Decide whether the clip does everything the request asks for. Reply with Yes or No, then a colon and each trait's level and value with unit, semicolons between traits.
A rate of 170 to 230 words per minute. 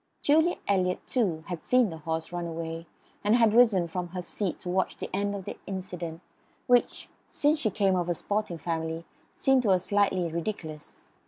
Yes: average, 185 wpm